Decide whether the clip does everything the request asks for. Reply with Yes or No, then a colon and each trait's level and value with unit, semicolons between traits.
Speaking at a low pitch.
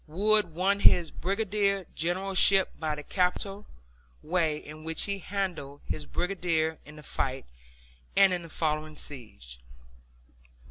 No: medium, 170 Hz